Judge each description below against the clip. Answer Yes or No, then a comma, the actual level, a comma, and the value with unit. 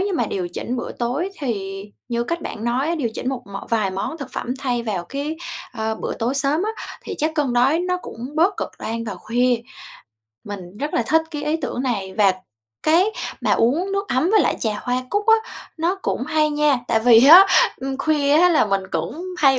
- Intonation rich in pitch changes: Yes, wide, 5.8 semitones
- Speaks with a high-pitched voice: Yes, very high, 260 Hz